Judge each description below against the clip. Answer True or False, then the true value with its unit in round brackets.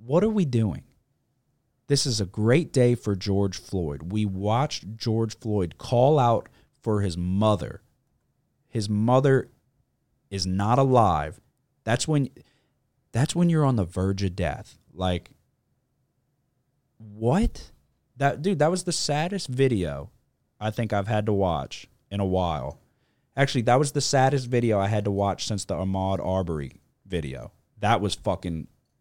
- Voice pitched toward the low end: True (115 Hz)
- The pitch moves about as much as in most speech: False (5.7 semitones)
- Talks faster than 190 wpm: False (150 wpm)